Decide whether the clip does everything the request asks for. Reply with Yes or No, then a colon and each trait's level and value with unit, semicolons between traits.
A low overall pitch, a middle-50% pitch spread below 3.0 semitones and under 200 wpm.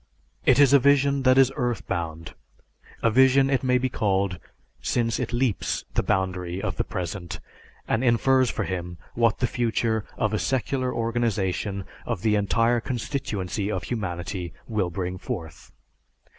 No: low, 110 Hz; average, 5.2 semitones; average, 155 wpm